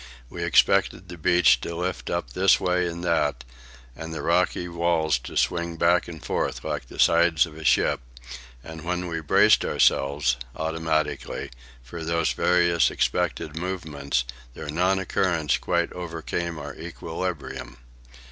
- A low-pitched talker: Yes, very low, 85 Hz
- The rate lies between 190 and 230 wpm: No, average, 145 wpm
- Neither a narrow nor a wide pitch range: No, narrow, 2.1 semitones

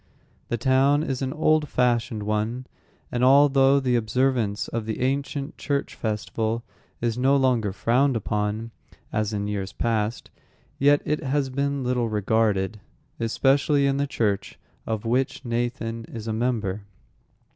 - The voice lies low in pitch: Yes, low, 120 Hz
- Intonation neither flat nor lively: Yes, average, 3.8 semitones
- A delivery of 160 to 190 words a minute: No, average, 140 wpm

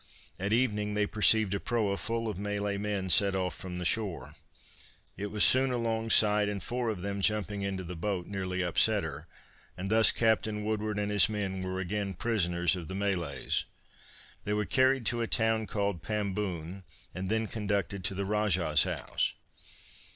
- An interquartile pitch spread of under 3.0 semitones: Yes, narrow, 2.5 semitones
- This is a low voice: Yes, low, 100 Hz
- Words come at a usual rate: Yes, average, 175 wpm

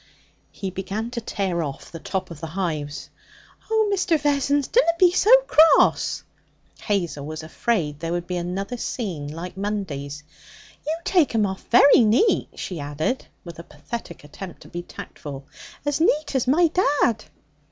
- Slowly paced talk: No, average, 160 wpm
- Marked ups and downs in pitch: Yes, wide, 9.0 semitones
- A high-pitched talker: Yes, high, 195 Hz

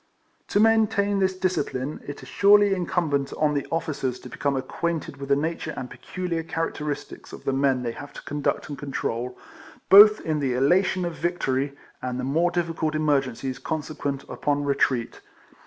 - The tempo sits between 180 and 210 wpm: No, average, 170 wpm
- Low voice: No, medium, 150 Hz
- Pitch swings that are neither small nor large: Yes, average, 4.2 semitones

